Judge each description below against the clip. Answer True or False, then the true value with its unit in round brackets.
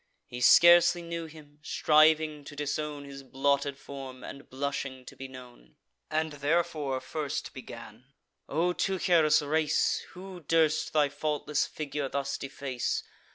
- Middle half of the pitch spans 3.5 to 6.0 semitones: False (2.4 semitones)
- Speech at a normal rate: False (130 wpm)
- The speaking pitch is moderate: True (145 Hz)